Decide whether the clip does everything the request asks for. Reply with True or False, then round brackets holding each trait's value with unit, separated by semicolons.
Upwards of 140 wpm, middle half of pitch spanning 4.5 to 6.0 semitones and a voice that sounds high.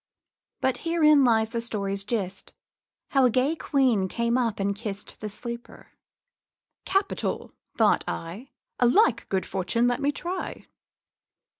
False (135 wpm; 5.3 semitones; 235 Hz)